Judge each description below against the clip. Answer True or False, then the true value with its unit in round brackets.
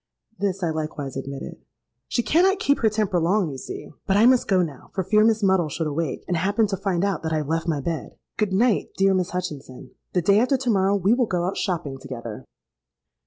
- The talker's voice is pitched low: False (185 Hz)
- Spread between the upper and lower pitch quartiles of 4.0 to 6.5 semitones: True (4.8 semitones)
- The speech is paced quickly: True (220 wpm)